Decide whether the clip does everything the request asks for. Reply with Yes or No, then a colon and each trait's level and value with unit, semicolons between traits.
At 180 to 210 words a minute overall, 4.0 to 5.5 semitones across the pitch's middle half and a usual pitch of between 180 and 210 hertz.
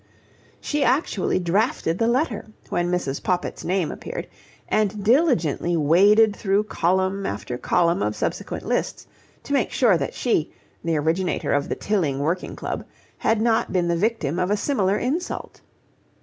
No: average, 150 wpm; average, 4.7 semitones; high, 190 Hz